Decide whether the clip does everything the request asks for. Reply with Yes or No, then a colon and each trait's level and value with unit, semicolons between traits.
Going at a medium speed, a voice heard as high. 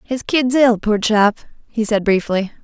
Yes: average, 180 wpm; high, 225 Hz